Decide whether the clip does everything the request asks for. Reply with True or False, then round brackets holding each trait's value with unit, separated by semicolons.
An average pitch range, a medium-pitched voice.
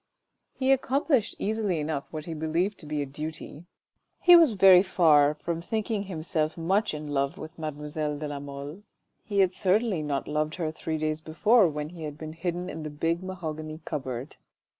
True (3.8 semitones; 160 Hz)